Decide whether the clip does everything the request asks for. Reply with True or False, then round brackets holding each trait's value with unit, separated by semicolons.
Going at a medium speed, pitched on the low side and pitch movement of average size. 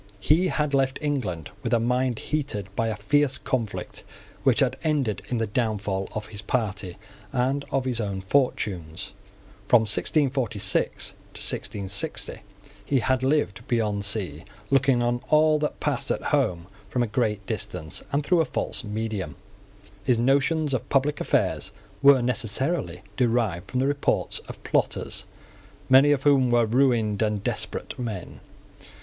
True (150 wpm; 120 Hz; 4.8 semitones)